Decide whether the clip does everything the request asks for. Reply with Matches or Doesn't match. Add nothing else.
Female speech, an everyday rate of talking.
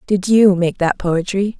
Matches